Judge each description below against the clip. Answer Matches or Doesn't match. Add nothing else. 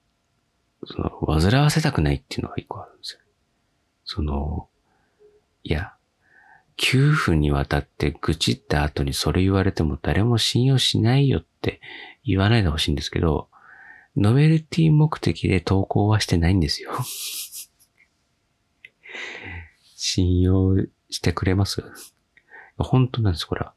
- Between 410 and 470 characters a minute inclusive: Doesn't match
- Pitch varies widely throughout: Matches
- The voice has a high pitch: Doesn't match